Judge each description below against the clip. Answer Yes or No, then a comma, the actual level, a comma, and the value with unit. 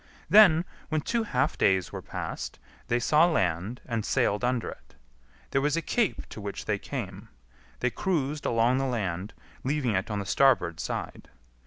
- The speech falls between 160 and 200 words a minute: Yes, average, 170 wpm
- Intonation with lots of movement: Yes, wide, 6.7 semitones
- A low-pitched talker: Yes, low, 125 Hz